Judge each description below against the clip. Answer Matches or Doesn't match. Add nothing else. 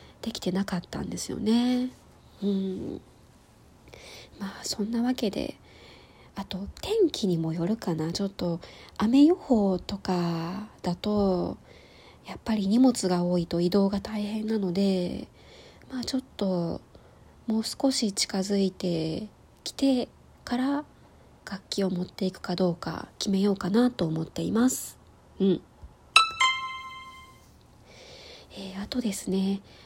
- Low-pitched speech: Doesn't match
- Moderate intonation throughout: Matches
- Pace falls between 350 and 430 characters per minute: Doesn't match